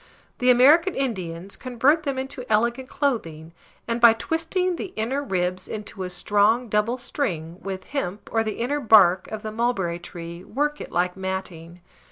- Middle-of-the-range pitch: No, high, 220 Hz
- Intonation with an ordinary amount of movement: No, wide, 6.1 semitones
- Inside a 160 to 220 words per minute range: Yes, average, 170 wpm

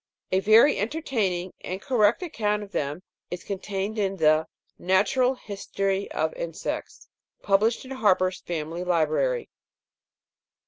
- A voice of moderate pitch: No, high, 195 Hz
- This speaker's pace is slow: Yes, slow, 125 wpm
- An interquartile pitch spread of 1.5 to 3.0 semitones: No, average, 3.7 semitones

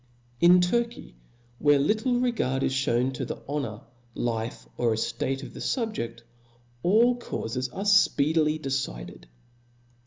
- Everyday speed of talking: No, slow, 125 wpm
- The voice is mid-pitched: Yes, medium, 145 Hz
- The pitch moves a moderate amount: No, wide, 8.7 semitones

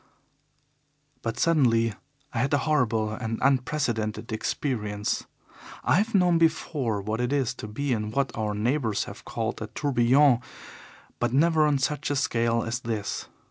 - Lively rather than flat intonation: No, average, 4.3 semitones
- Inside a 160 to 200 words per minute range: No, average, 150 wpm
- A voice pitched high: No, low, 125 Hz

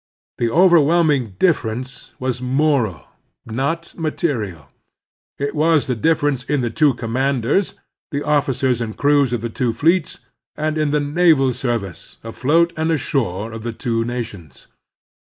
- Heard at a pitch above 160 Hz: No, low, 135 Hz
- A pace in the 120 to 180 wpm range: Yes, average, 140 wpm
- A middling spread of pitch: Yes, average, 4.7 semitones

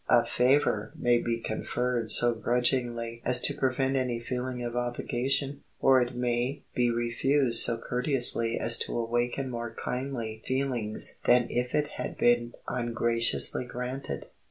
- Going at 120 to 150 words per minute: Yes, average, 140 wpm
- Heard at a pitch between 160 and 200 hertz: No, low, 120 Hz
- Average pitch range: No, narrow, 1.5 semitones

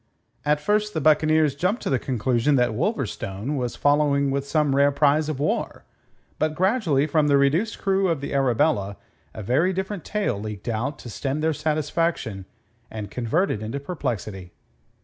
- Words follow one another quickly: No, average, 170 wpm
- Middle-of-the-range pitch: Yes, medium, 145 Hz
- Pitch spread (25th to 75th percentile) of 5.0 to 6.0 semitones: No, average, 4.4 semitones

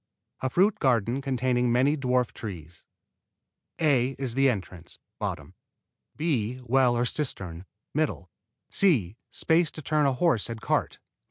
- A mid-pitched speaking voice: No, low, 125 Hz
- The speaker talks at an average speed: No, slow, 125 wpm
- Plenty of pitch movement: No, average, 3.4 semitones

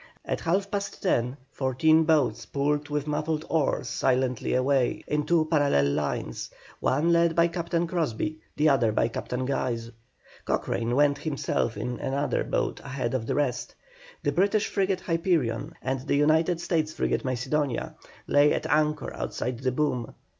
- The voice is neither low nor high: Yes, medium, 145 Hz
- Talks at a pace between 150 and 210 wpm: Yes, average, 155 wpm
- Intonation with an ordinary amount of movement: Yes, average, 4.0 semitones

